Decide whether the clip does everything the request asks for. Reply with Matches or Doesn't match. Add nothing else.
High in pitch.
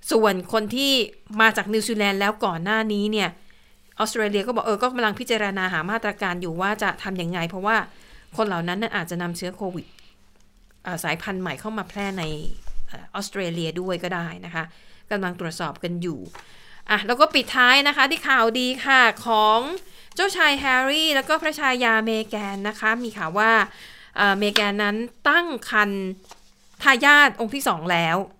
Matches